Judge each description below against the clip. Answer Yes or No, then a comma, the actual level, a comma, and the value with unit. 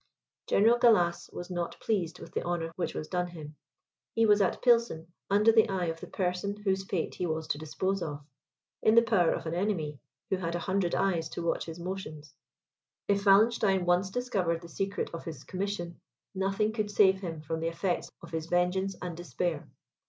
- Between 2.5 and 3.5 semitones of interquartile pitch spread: Yes, average, 3.1 semitones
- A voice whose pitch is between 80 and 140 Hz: No, medium, 180 Hz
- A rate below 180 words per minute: No, average, 195 wpm